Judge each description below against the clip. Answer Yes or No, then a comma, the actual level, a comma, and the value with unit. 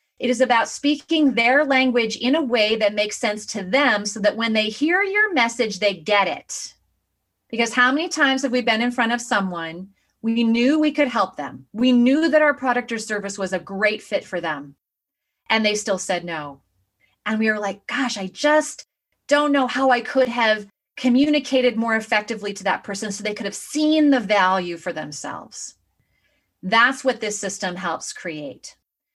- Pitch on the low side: No, high, 230 Hz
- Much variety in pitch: No, average, 4.9 semitones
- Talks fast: No, average, 190 wpm